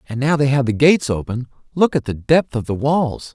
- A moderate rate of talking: No, fast, 250 wpm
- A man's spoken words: Yes, male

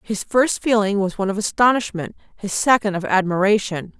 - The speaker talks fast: No, average, 165 wpm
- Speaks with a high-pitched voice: Yes, high, 205 Hz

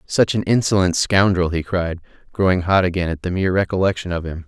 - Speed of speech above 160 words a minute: Yes, average, 200 wpm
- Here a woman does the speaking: No, male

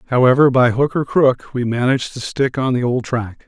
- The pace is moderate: No, fast, 225 wpm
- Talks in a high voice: No, low, 125 Hz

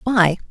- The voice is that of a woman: Yes, female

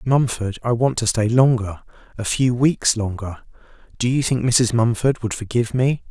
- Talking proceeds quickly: No, average, 165 wpm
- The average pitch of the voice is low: Yes, low, 115 Hz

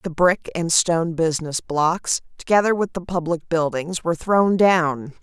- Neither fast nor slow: Yes, average, 160 wpm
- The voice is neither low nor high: Yes, medium, 170 Hz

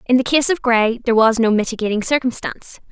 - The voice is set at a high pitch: Yes, high, 235 Hz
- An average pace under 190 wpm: No, fast, 205 wpm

